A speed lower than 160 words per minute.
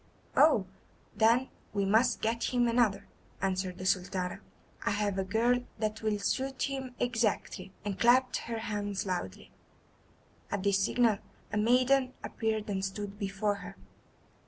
Yes: average, 140 wpm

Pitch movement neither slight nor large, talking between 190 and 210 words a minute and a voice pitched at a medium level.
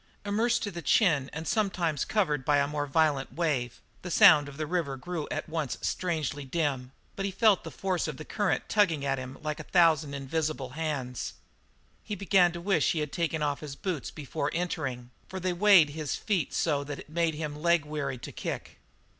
Yes: average, 3.8 semitones; fast, 205 wpm; medium, 155 Hz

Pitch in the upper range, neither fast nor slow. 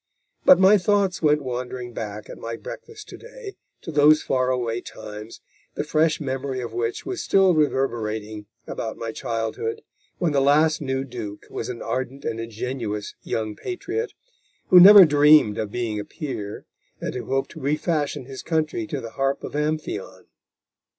No: low, 135 Hz; average, 165 wpm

